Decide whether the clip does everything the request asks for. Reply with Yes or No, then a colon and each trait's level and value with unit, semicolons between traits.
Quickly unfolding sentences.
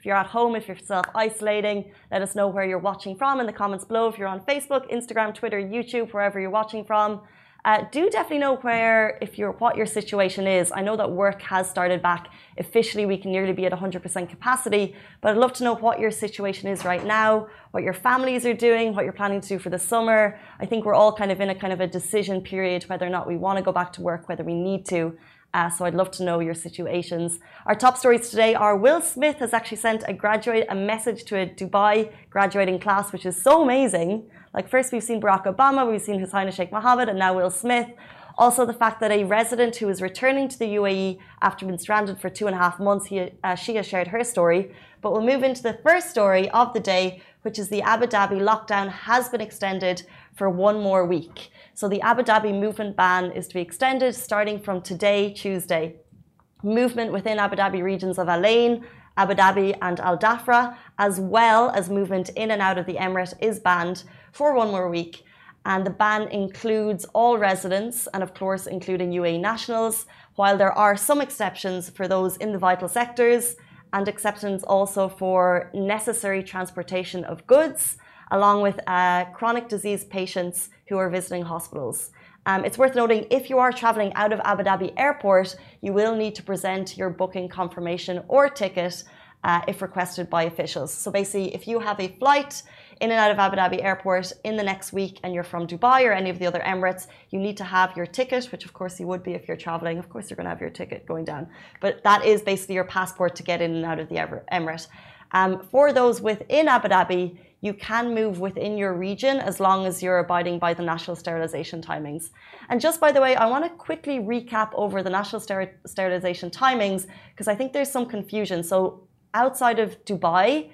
Yes: fast, 215 wpm